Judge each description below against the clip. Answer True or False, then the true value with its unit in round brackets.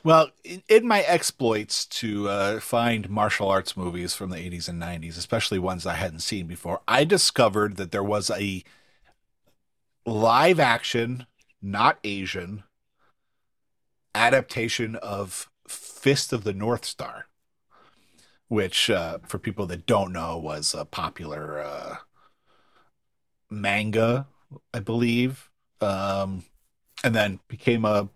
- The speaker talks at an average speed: False (120 wpm)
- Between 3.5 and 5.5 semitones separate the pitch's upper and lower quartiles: True (4.1 semitones)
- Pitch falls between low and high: False (105 Hz)